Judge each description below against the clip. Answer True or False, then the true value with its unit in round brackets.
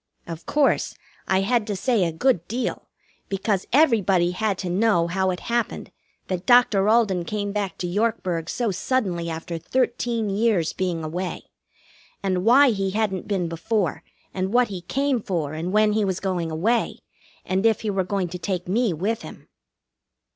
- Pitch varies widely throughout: False (4.1 semitones)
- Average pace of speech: True (170 wpm)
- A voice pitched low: False (195 Hz)